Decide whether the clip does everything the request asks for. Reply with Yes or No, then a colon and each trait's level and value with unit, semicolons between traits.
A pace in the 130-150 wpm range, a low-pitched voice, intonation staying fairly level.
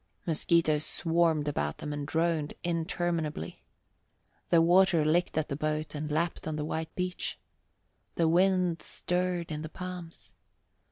No: slow, 135 wpm; medium, 165 Hz; narrow, 2.2 semitones